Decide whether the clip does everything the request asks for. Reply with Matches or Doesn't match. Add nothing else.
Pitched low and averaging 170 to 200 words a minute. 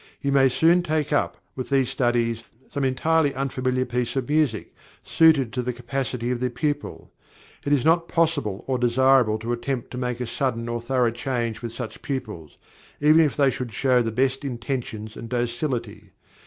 Matches